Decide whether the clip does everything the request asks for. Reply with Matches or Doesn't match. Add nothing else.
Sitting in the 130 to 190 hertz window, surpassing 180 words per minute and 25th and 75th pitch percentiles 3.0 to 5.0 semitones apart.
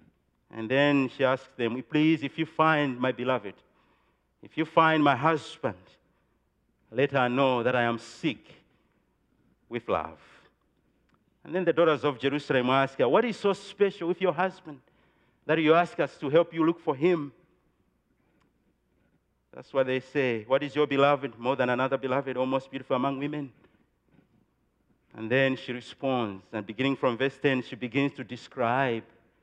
Doesn't match